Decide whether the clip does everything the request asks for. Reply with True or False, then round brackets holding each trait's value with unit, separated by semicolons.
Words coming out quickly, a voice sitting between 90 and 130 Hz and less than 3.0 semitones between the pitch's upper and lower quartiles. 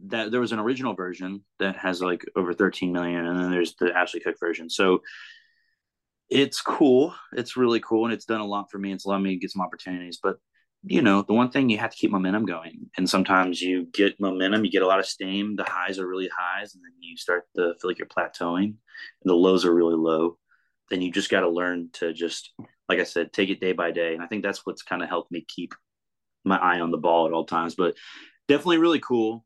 False (245 wpm; 95 Hz; 3.7 semitones)